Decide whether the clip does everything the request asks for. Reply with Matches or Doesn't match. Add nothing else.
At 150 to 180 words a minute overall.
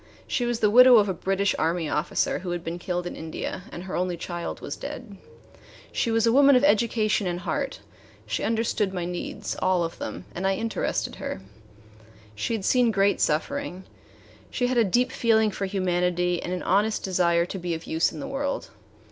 Doesn't match